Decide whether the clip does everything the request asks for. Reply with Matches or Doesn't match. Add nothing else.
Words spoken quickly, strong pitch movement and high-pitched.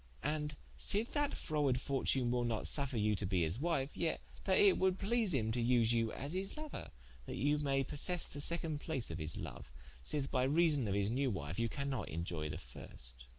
Doesn't match